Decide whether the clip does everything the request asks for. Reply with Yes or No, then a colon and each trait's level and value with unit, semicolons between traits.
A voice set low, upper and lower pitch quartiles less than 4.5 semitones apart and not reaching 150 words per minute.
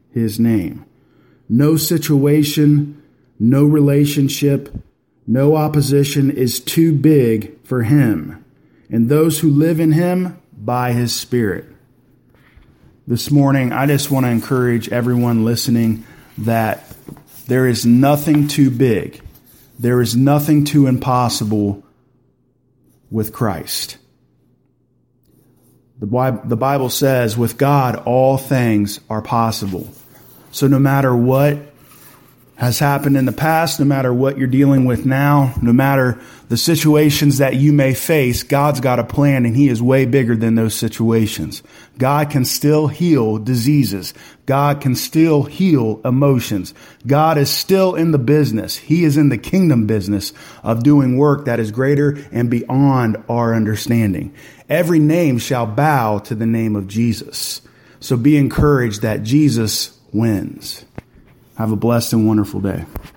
Yes: low, 130 Hz; average, 3.8 semitones; slow, 135 wpm